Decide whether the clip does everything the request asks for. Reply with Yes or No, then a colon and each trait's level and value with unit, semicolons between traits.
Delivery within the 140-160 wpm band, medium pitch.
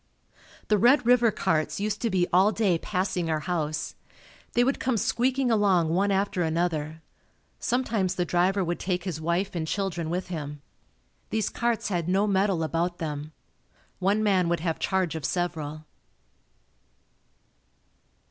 Yes: average, 150 wpm; medium, 180 Hz